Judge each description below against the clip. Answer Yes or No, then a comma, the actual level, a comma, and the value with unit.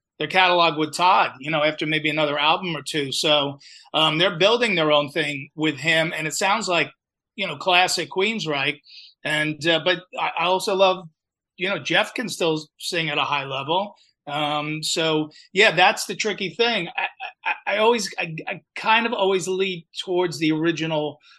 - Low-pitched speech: No, medium, 160 Hz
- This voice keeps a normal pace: Yes, average, 180 wpm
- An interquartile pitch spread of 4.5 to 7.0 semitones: No, average, 3.6 semitones